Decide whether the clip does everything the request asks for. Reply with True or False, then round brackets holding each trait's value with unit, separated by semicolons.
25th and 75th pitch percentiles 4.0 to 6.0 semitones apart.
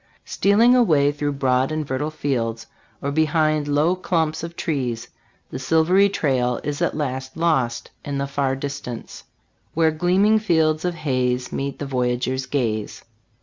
False (3.6 semitones)